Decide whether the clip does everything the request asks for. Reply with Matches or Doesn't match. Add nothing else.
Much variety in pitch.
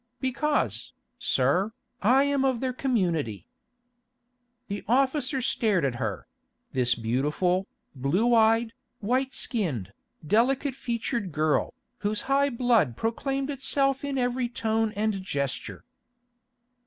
Matches